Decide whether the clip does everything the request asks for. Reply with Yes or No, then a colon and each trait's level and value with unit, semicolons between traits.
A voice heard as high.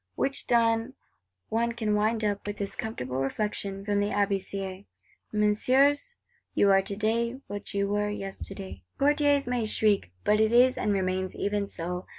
Yes: high, 210 Hz